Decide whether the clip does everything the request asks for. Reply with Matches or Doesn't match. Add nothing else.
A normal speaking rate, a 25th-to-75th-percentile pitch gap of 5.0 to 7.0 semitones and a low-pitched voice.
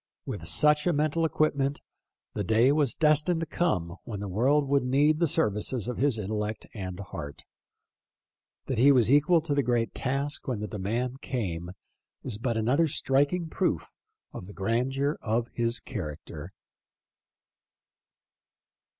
Matches